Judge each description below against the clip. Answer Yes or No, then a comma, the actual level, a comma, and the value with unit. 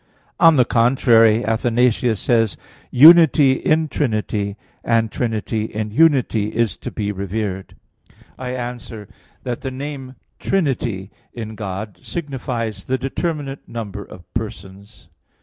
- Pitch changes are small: No, average, 3.7 semitones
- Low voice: Yes, low, 115 Hz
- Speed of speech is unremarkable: No, slow, 115 wpm